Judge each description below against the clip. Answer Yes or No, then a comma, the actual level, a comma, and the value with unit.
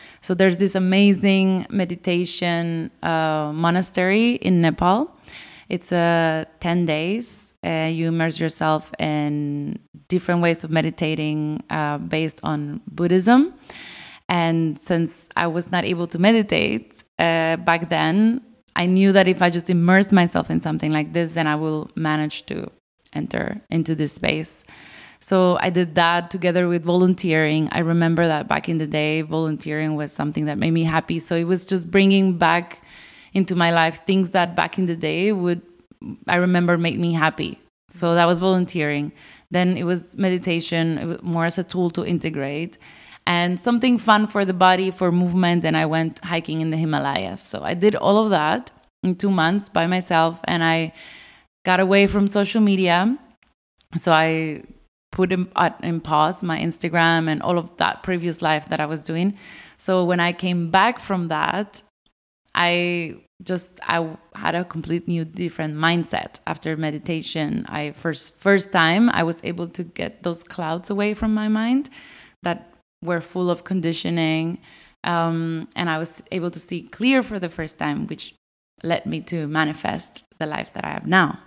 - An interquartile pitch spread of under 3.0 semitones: Yes, narrow, 2.4 semitones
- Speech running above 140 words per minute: Yes, average, 165 wpm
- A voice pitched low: No, medium, 170 Hz